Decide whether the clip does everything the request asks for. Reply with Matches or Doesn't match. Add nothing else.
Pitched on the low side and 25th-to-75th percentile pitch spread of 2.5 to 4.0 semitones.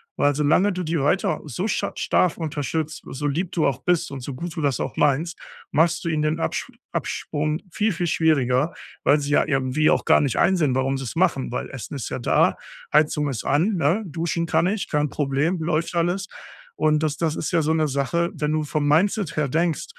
Doesn't match